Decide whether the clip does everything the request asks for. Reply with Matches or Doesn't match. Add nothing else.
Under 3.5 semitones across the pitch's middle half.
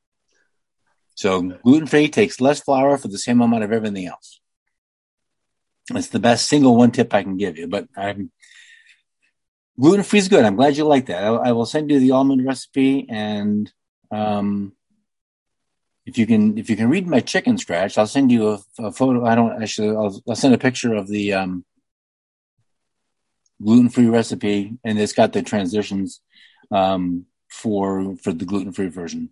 Doesn't match